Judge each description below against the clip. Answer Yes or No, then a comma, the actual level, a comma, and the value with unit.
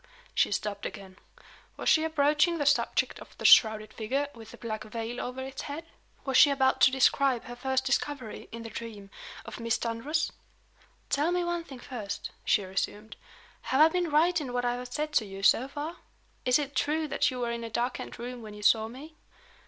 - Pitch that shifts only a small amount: No, average, 4.4 semitones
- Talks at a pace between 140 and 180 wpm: No, fast, 205 wpm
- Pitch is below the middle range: No, very high, 250 Hz